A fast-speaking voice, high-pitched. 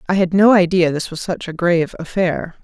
No: fast, 230 wpm; medium, 175 Hz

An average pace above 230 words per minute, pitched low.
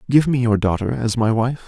Yes: fast, 250 wpm; low, 115 Hz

